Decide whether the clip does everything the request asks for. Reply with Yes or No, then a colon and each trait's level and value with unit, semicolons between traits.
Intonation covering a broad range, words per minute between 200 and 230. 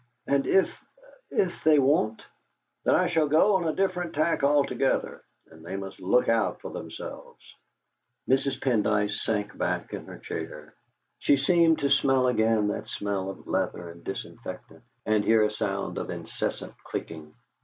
No: wide, 6.5 semitones; average, 155 wpm